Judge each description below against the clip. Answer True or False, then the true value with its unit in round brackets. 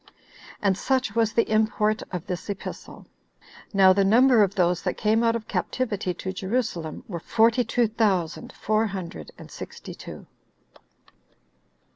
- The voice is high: True (210 Hz)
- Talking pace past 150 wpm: False (145 wpm)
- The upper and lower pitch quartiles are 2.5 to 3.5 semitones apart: True (3.2 semitones)